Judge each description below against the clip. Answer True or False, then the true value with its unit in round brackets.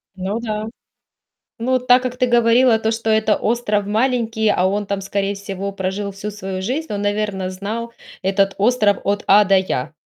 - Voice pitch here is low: False (210 Hz)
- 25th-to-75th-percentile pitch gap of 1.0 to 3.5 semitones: True (2.8 semitones)